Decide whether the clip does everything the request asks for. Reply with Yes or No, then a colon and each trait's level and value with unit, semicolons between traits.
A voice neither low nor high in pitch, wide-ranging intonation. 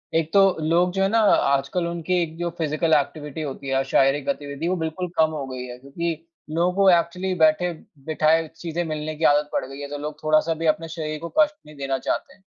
No: medium, 155 Hz; average, 2.7 semitones